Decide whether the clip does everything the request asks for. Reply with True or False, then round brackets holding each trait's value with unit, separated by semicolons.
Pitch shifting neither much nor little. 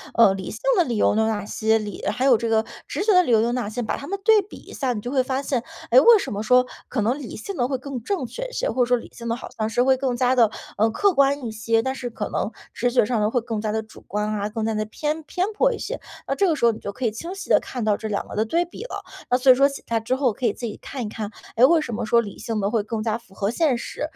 True (3.9 semitones)